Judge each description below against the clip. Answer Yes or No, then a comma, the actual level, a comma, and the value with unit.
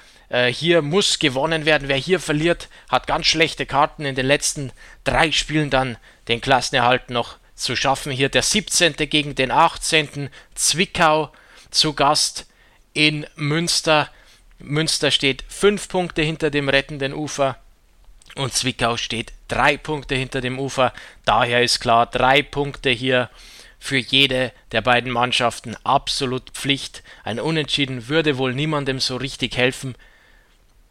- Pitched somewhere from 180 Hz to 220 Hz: No, medium, 140 Hz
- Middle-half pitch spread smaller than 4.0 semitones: Yes, average, 3.3 semitones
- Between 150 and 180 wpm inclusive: No, average, 135 wpm